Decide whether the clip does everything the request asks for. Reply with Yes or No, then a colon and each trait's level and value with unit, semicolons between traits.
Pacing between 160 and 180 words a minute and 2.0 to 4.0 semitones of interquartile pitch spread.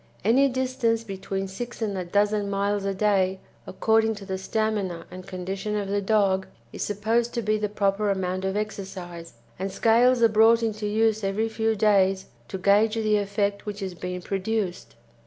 Yes: average, 175 wpm; narrow, 2.4 semitones